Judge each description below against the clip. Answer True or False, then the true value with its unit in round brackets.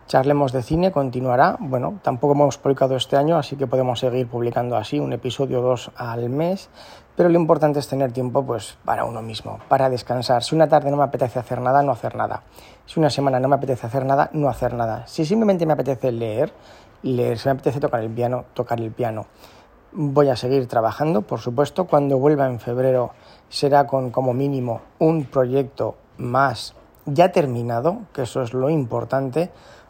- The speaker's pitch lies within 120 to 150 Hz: True (135 Hz)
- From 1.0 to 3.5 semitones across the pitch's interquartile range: True (2.9 semitones)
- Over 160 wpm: True (190 wpm)